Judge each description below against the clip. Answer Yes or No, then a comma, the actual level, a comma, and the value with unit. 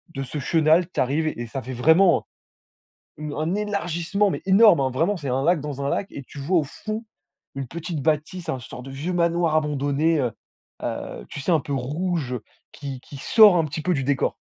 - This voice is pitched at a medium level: Yes, medium, 155 Hz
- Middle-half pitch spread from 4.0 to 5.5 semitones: Yes, average, 4.3 semitones